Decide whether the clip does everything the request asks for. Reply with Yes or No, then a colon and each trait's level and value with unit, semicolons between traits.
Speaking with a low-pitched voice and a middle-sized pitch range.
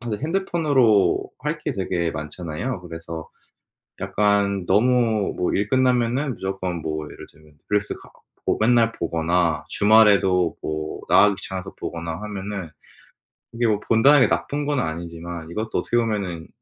No: low, 100 Hz; wide, 5.7 semitones